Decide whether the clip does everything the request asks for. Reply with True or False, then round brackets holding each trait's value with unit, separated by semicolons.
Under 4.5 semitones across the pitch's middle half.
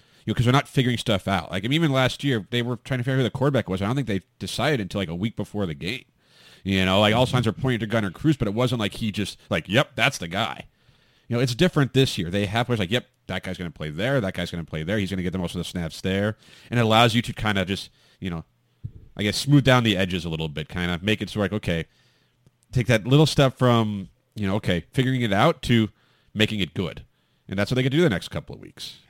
False (4.8 semitones)